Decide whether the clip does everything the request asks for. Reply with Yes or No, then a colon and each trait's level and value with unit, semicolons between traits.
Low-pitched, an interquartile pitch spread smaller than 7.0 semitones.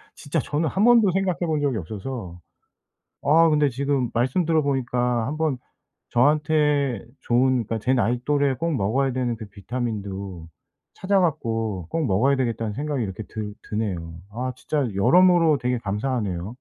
Yes: low, 130 Hz; average, 5.3 semitones